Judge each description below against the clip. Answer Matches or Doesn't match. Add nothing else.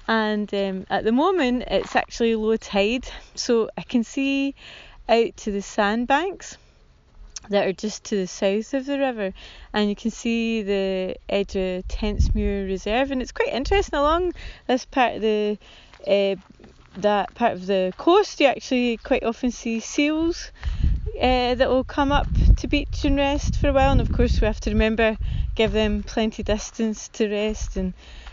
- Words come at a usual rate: Matches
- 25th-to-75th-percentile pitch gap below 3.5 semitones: Doesn't match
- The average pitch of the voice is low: Doesn't match